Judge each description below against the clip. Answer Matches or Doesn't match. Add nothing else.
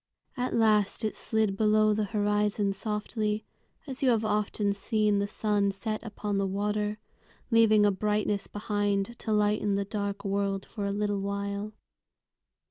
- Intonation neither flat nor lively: Doesn't match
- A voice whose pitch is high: Matches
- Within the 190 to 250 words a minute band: Doesn't match